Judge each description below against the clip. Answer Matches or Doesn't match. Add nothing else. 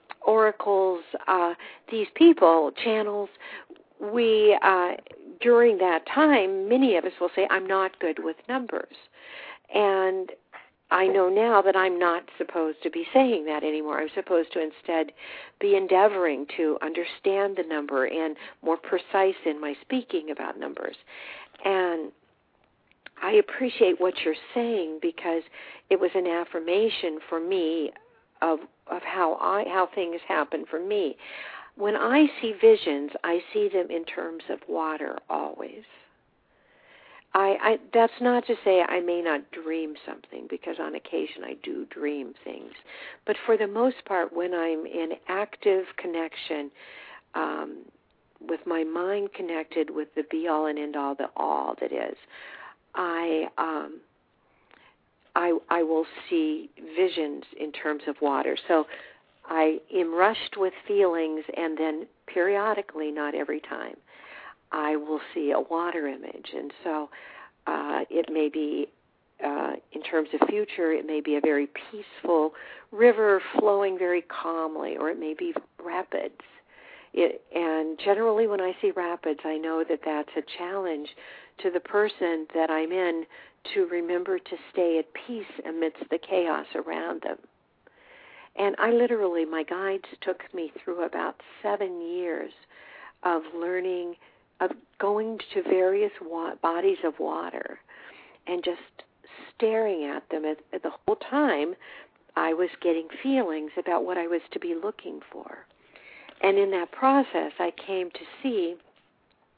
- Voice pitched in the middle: Matches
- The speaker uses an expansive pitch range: Doesn't match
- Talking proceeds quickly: Doesn't match